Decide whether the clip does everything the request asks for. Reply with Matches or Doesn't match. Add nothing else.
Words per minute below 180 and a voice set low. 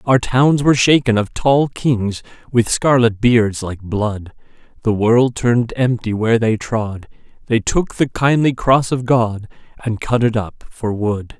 Matches